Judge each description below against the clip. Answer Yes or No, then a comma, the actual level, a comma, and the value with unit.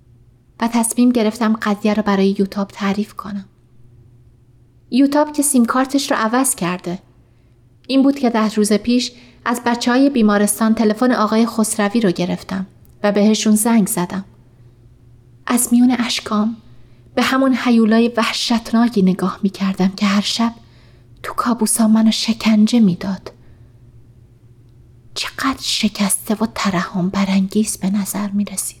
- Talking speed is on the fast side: No, average, 130 wpm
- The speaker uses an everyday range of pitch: Yes, average, 5.0 semitones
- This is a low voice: No, high, 205 Hz